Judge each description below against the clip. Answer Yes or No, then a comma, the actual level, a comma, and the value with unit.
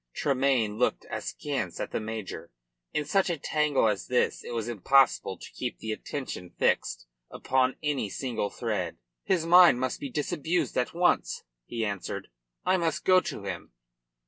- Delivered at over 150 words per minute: Yes, average, 160 wpm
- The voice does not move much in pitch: No, wide, 5.5 semitones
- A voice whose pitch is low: Yes, low, 130 Hz